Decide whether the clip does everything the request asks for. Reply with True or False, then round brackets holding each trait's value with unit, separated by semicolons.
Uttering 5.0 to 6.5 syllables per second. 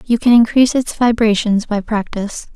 True (5.4 syllables/s)